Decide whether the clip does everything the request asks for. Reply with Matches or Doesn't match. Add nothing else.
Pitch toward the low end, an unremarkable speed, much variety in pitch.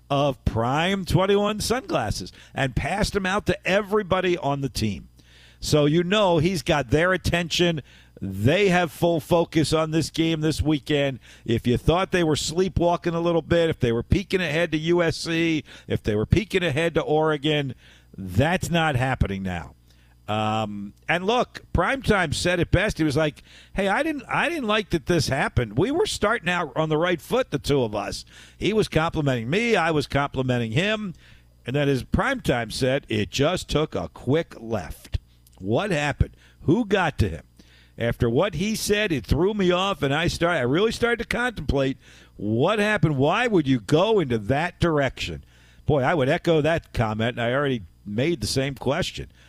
Doesn't match